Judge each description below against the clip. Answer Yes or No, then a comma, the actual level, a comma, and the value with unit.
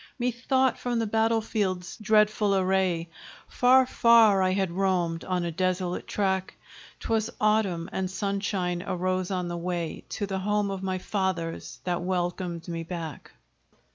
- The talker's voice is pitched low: No, high, 190 Hz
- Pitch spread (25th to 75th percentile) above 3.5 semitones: No, average, 3.0 semitones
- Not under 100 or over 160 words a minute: Yes, average, 145 wpm